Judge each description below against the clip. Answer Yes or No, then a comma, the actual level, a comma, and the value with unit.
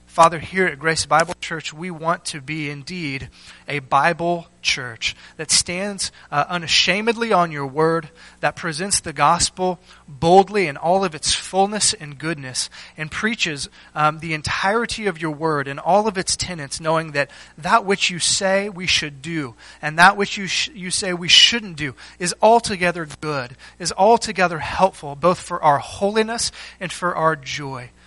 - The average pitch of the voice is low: No, medium, 170 Hz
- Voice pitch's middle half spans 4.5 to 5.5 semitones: No, average, 3.8 semitones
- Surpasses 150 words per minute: Yes, average, 170 wpm